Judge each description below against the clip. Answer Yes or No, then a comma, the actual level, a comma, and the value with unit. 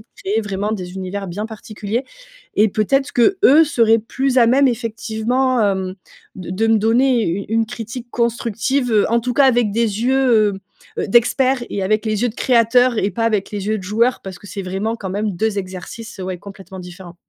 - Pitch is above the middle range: Yes, high, 220 Hz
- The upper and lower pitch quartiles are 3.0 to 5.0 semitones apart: Yes, average, 3.3 semitones